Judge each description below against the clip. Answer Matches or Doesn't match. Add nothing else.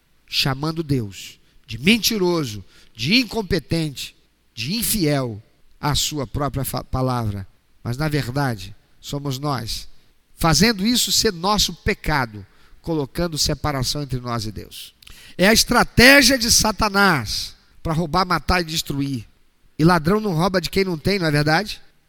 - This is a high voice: Doesn't match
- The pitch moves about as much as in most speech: Doesn't match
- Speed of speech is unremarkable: Matches